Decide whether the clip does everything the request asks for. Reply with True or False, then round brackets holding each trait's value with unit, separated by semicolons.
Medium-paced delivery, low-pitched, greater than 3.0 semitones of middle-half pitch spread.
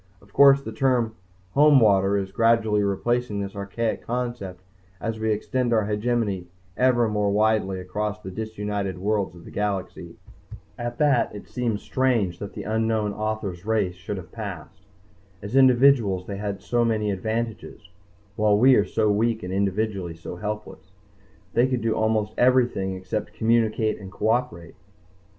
False (150 wpm; 105 Hz; 2.7 semitones)